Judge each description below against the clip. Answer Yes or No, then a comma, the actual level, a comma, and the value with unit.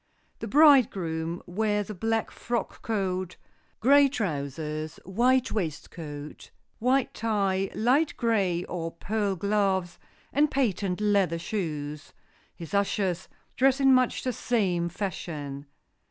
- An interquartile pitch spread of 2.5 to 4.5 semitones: No, average, 5.2 semitones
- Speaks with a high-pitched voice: Yes, high, 195 Hz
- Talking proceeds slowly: Yes, slow, 110 wpm